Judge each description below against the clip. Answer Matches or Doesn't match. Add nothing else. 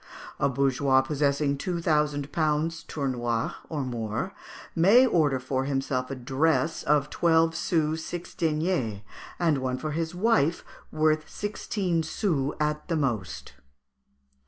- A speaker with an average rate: Doesn't match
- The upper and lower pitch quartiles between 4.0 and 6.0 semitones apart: Doesn't match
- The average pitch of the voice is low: Doesn't match